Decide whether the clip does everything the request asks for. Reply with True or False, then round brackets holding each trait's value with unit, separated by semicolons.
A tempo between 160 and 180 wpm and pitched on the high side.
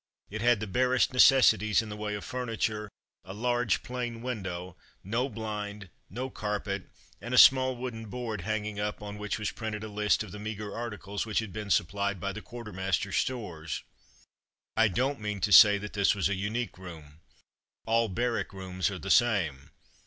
False (175 wpm; 105 Hz)